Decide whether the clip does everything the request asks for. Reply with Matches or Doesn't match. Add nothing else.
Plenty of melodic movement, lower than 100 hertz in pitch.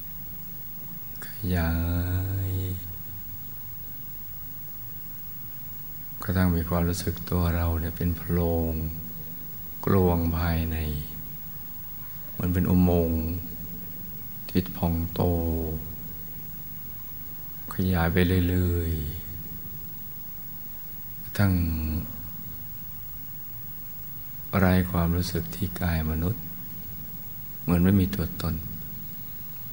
Doesn't match